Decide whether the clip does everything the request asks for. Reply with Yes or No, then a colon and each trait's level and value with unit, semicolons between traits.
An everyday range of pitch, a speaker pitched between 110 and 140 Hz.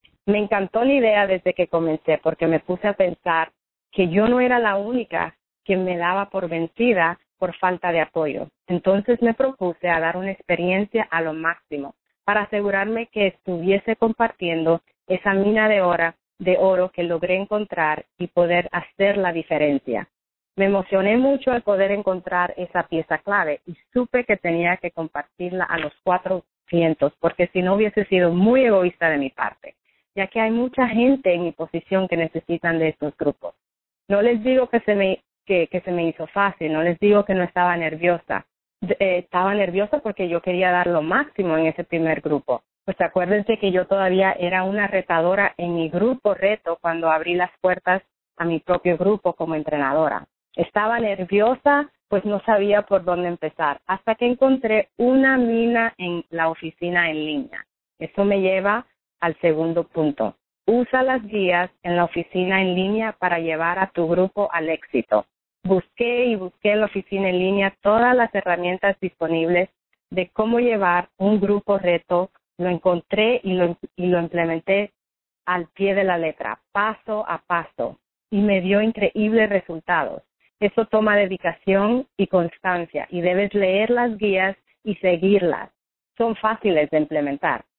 No: average, 3.3 semitones; medium, 185 Hz